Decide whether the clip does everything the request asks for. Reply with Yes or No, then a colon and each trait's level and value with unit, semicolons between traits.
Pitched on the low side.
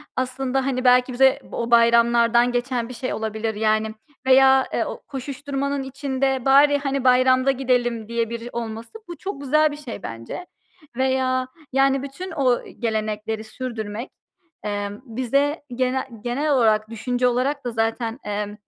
No: very high, 250 Hz